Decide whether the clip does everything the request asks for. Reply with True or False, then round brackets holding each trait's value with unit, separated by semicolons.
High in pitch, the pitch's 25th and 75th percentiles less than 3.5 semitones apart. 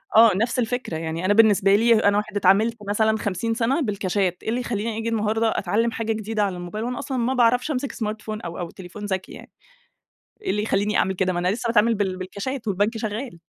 True (215 Hz; 2.8 semitones)